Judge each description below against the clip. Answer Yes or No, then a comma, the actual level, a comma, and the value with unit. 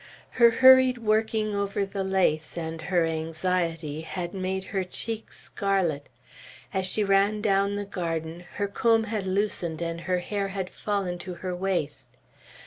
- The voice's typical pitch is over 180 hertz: Yes, high, 190 Hz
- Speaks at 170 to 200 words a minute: No, average, 145 wpm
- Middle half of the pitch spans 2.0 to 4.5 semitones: Yes, average, 3.2 semitones